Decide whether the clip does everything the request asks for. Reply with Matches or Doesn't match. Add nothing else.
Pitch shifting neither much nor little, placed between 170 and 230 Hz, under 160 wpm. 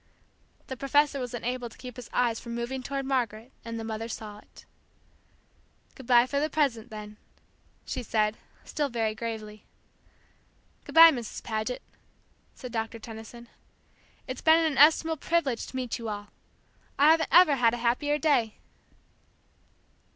Doesn't match